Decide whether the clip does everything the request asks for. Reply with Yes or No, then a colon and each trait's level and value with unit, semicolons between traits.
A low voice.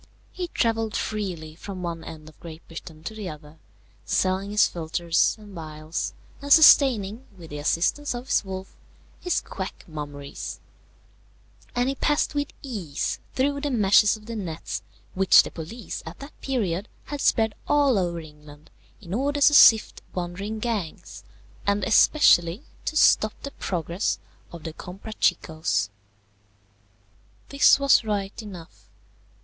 No: high, 195 Hz